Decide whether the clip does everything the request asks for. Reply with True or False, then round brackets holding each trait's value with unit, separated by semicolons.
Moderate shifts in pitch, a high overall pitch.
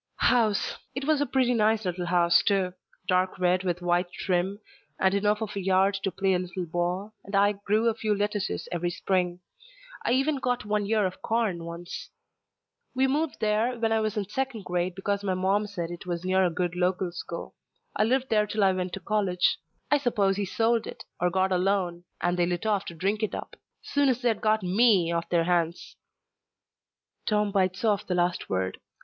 True (3.3 semitones; 195 Hz)